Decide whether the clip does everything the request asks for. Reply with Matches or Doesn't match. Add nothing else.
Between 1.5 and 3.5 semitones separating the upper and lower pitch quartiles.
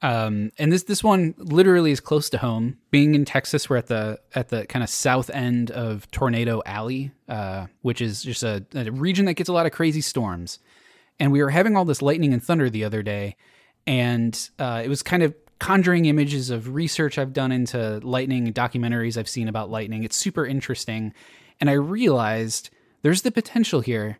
Doesn't match